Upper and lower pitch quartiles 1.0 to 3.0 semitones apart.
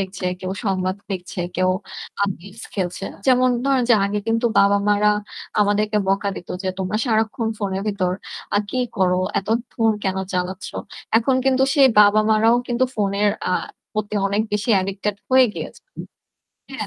Yes: average, 2.7 semitones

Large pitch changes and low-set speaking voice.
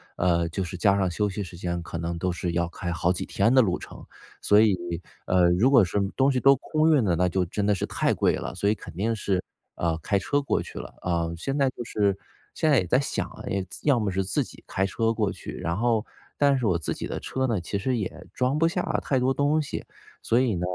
Yes: wide, 6.2 semitones; low, 100 Hz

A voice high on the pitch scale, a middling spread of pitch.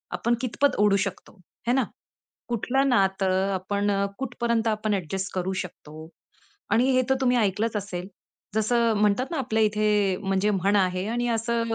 Yes: high, 210 Hz; average, 3.5 semitones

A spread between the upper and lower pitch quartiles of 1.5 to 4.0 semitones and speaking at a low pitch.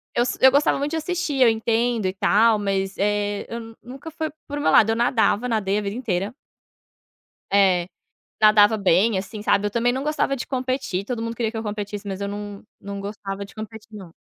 No: average, 3.4 semitones; high, 215 Hz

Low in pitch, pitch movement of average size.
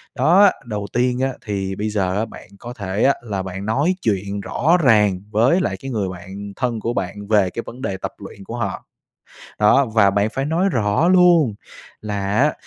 Yes: low, 110 Hz; average, 4.8 semitones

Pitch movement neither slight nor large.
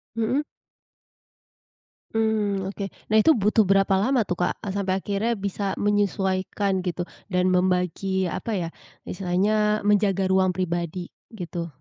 No: narrow, 2.2 semitones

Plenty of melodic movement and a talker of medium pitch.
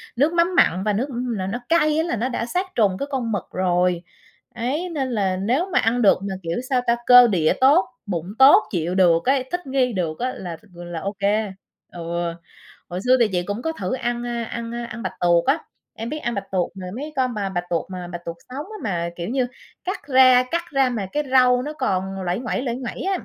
No: wide, 6.2 semitones; high, 235 Hz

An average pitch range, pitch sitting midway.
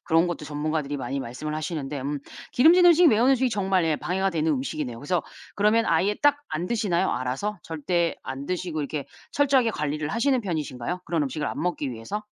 No: wide, 6.0 semitones; medium, 165 Hz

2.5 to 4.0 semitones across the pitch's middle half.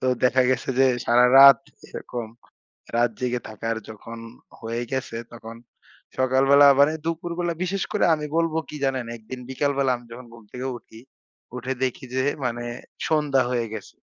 Yes: average, 2.9 semitones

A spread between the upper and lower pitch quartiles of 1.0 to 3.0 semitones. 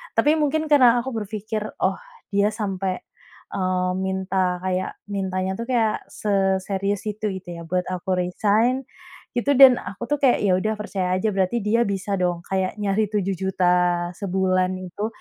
Yes: average, 2.7 semitones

